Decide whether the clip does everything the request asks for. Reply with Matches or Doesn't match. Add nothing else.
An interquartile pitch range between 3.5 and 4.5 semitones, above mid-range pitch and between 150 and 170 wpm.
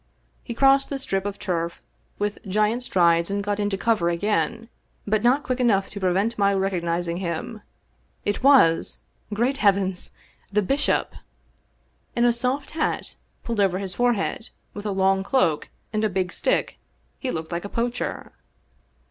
Matches